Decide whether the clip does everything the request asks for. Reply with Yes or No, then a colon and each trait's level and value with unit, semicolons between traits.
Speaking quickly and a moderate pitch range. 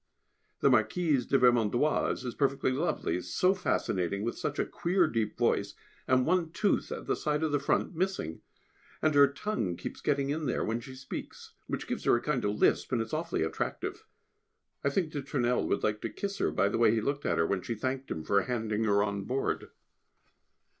No: fast, 210 wpm; wide, 5.7 semitones